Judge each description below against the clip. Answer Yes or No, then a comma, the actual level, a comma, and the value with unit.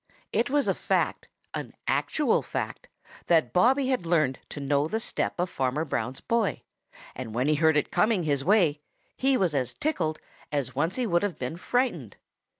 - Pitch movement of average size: No, wide, 7.9 semitones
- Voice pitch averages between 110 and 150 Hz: No, medium, 165 Hz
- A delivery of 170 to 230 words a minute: Yes, average, 180 wpm